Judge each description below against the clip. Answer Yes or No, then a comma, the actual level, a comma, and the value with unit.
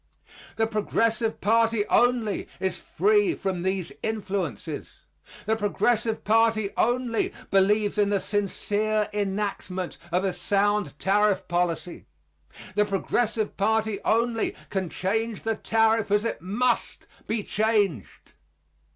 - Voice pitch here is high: Yes, high, 210 Hz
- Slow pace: Yes, slow, 115 wpm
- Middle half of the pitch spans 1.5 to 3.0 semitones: Yes, narrow, 2.4 semitones